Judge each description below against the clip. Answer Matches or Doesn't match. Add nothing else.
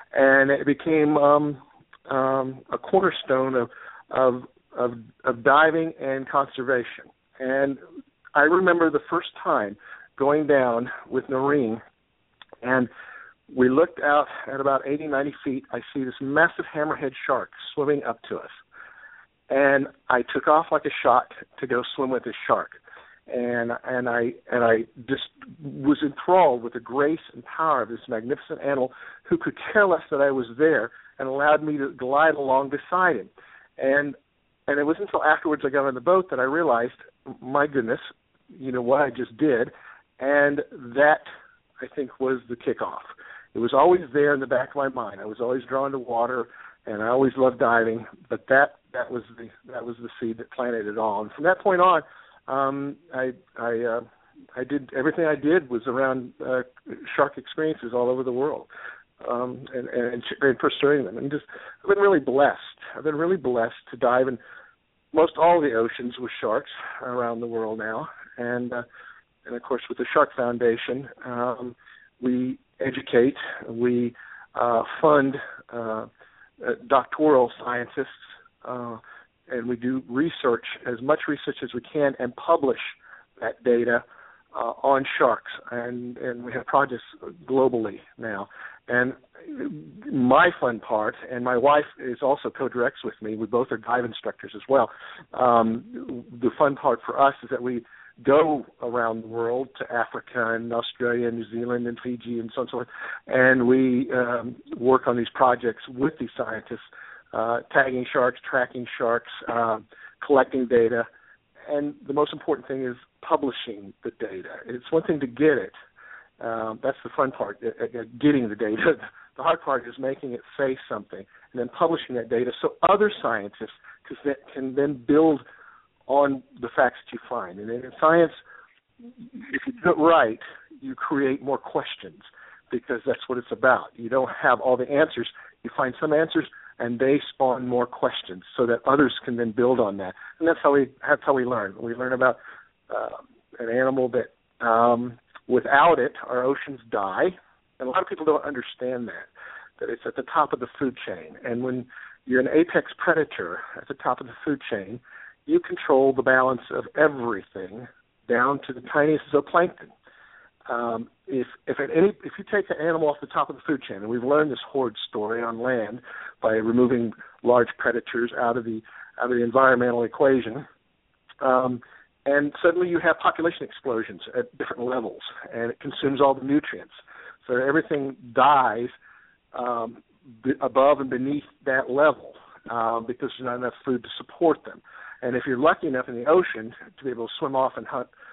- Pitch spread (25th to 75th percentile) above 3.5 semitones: Doesn't match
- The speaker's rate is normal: Matches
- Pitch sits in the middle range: Doesn't match